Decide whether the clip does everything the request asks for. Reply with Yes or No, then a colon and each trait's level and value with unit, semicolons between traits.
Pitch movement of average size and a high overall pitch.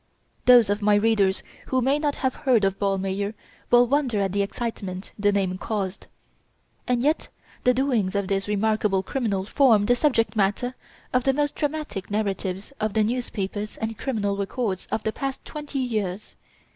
Yes: average, 4.1 semitones; high, 215 Hz